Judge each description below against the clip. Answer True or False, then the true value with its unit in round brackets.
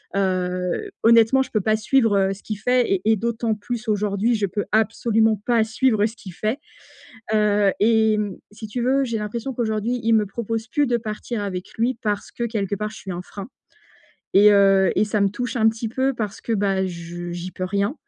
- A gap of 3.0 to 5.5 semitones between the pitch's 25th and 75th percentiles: False (2.6 semitones)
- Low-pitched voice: False (215 Hz)